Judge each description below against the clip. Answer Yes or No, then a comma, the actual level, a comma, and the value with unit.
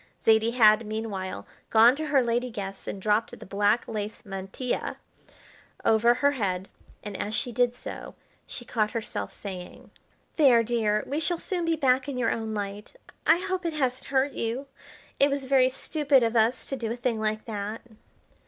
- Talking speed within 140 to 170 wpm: No, average, 180 wpm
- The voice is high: Yes, high, 230 Hz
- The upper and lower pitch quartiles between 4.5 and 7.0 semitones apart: No, average, 3.8 semitones